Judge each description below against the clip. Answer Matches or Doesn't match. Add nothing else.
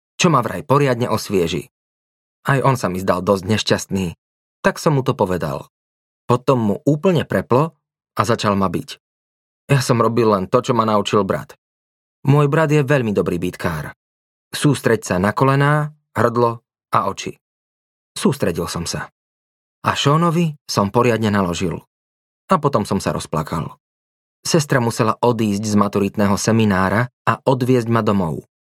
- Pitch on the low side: Matches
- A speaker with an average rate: Matches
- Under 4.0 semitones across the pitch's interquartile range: Doesn't match